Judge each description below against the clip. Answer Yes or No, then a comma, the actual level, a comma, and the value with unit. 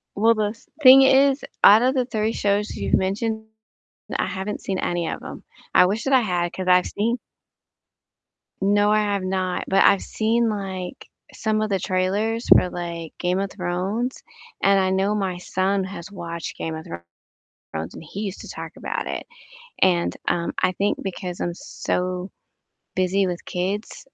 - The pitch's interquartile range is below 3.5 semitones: Yes, average, 2.8 semitones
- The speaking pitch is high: Yes, high, 195 Hz